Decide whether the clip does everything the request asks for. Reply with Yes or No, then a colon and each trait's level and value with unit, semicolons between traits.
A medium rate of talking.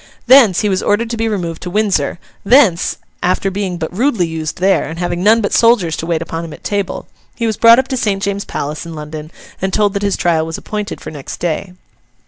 No: fast, 230 wpm